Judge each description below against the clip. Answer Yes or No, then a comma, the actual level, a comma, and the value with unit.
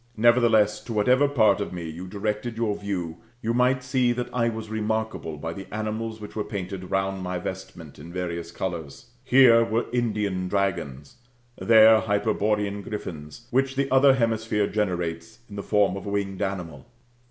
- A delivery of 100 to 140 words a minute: No, average, 165 wpm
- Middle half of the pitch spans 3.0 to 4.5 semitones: Yes, average, 3.7 semitones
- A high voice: No, low, 105 Hz